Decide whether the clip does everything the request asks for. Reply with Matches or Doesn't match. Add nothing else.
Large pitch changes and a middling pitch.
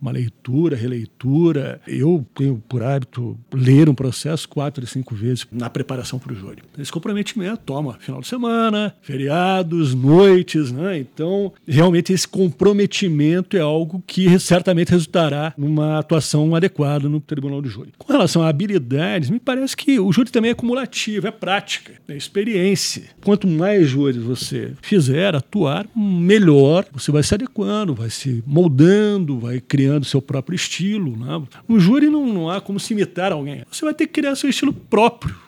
Matches